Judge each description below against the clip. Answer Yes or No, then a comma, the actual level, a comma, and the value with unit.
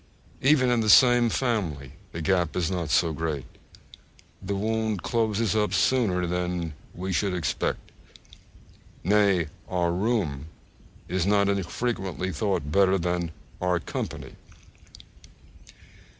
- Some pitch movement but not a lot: Yes, average, 3.8 semitones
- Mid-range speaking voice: No, very low, 95 Hz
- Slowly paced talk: Yes, slow, 115 wpm